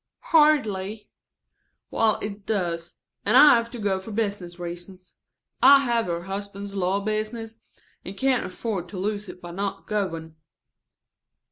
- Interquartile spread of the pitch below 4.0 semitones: Yes, average, 3.5 semitones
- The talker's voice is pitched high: Yes, high, 200 Hz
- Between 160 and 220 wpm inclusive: No, average, 140 wpm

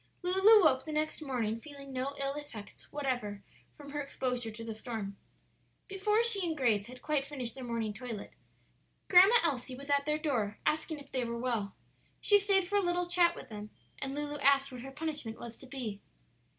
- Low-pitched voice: No, very high, 275 Hz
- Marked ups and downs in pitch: No, average, 4.8 semitones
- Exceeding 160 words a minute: Yes, average, 195 wpm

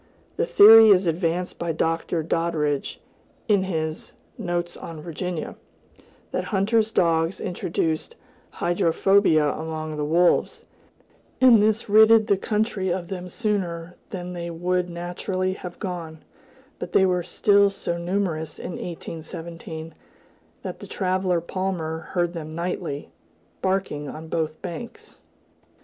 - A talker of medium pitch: Yes, medium, 175 Hz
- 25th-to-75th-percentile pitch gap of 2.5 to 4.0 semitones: Yes, average, 2.9 semitones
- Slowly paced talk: Yes, slow, 125 wpm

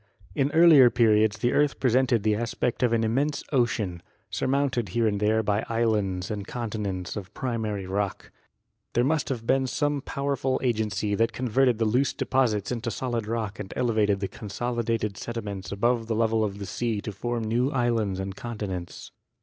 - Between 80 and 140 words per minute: No, average, 170 wpm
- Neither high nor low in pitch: No, low, 115 Hz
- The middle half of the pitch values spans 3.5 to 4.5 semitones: No, average, 3.1 semitones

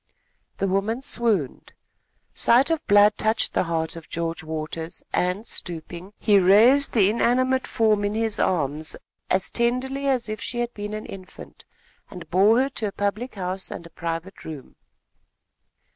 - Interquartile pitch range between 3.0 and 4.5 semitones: No, average, 5.1 semitones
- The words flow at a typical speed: Yes, average, 160 wpm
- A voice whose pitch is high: Yes, high, 205 Hz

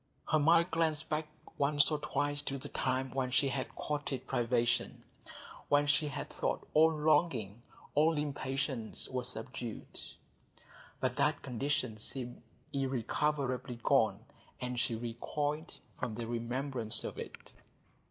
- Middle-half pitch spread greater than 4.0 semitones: No, average, 3.3 semitones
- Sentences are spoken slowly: Yes, slow, 130 wpm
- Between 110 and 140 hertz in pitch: Yes, low, 135 Hz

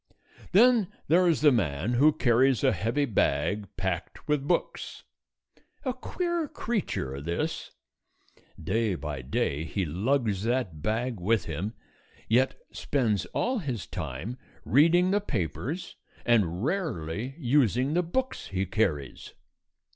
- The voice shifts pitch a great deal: Yes, wide, 8.9 semitones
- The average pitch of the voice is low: Yes, low, 120 Hz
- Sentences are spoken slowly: Yes, slow, 125 wpm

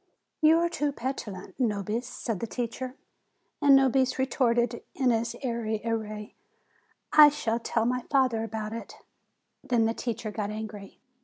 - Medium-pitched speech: No, high, 235 Hz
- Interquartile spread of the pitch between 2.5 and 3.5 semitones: Yes, average, 3.0 semitones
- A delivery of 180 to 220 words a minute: No, average, 155 wpm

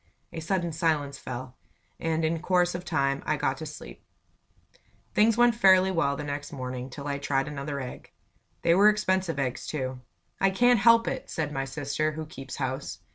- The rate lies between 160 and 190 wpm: Yes, average, 180 wpm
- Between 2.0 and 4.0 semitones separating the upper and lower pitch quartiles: No, average, 5.0 semitones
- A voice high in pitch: No, medium, 155 Hz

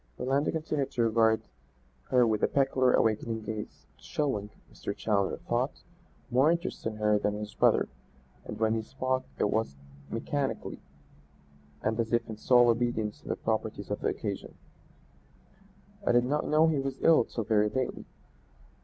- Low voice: Yes, low, 115 Hz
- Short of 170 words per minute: Yes, average, 160 wpm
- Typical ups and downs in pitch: Yes, average, 3.6 semitones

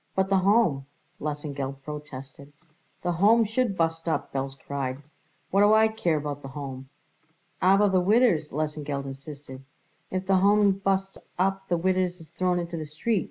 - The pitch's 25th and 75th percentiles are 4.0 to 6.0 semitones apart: Yes, average, 5.2 semitones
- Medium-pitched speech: Yes, medium, 170 Hz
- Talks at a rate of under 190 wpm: Yes, average, 160 wpm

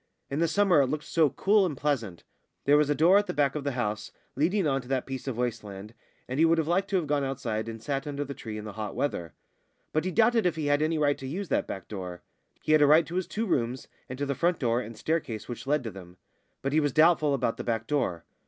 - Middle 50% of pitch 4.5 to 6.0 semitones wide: Yes, average, 5.3 semitones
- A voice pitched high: No, medium, 140 Hz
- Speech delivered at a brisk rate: Yes, fast, 275 wpm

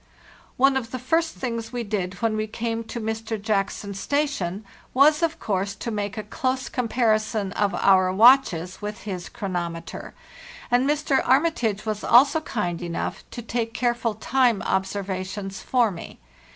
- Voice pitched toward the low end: No, high, 220 Hz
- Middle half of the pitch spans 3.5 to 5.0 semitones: Yes, average, 4.1 semitones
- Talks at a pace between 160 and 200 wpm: No, average, 150 wpm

